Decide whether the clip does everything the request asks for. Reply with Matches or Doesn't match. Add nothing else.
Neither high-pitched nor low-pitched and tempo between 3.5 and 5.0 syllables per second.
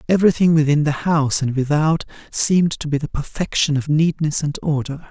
Doesn't match